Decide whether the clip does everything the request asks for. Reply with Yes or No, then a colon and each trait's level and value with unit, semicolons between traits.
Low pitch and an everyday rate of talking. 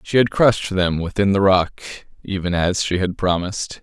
Yes: very low, 95 Hz; average, 170 wpm